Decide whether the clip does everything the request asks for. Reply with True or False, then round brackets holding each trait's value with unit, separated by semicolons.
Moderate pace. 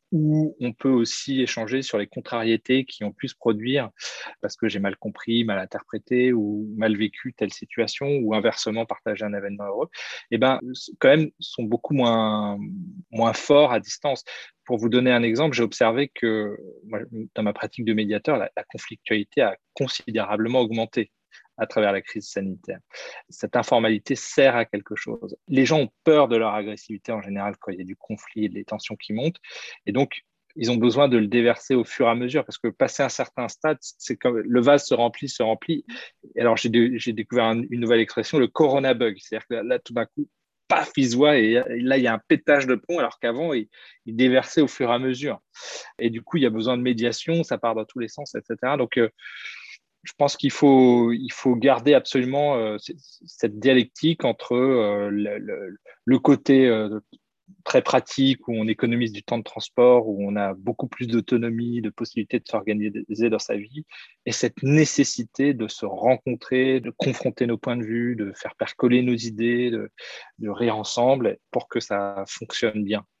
True (200 wpm)